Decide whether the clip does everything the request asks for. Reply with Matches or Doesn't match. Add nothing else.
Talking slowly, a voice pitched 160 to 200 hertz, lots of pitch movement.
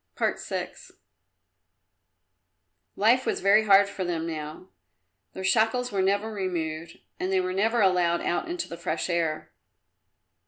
Doesn't match